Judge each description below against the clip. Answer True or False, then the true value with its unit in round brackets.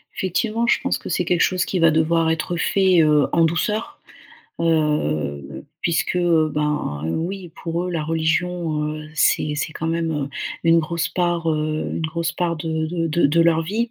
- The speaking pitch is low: False (165 Hz)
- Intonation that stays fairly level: True (2.0 semitones)